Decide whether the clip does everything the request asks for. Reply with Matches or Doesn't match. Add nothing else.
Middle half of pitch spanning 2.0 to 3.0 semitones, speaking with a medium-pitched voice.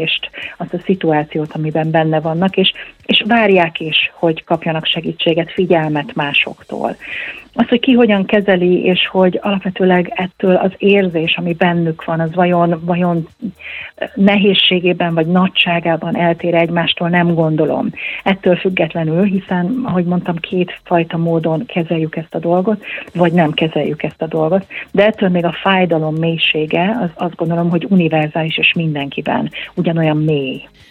Matches